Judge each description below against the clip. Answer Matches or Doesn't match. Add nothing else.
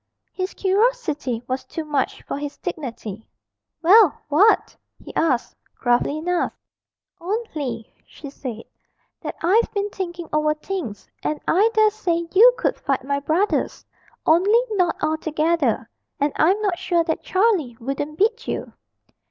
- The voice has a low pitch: Doesn't match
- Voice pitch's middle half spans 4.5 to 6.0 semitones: Matches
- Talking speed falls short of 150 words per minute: Matches